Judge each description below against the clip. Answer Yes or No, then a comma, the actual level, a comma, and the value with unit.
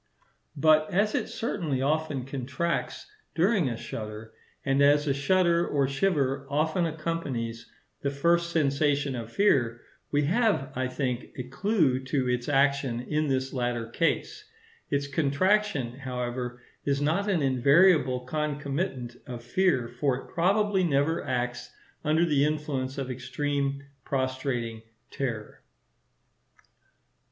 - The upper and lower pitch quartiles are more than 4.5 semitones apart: No, average, 3.9 semitones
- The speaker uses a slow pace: Yes, slow, 125 wpm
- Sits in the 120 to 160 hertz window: Yes, medium, 140 Hz